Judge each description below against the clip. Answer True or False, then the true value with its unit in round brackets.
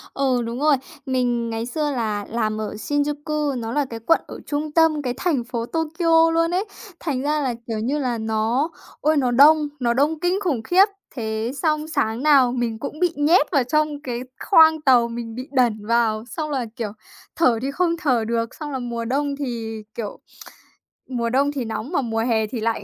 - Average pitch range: True (4.6 semitones)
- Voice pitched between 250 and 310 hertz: True (260 Hz)